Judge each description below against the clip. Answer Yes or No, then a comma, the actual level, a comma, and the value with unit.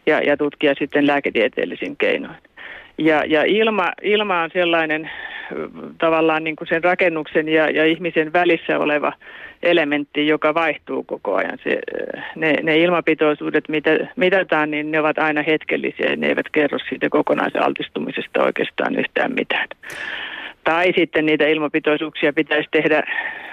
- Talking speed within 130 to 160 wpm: Yes, average, 135 wpm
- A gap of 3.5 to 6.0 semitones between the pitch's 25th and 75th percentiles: No, narrow, 2.6 semitones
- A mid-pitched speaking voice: Yes, medium, 160 Hz